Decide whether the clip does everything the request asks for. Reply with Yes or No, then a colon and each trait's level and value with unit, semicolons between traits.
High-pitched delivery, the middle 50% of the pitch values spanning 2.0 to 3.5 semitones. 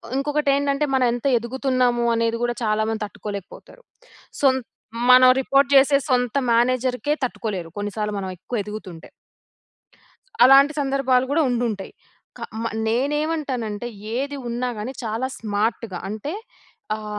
No: high, 245 Hz; average, 4.0 semitones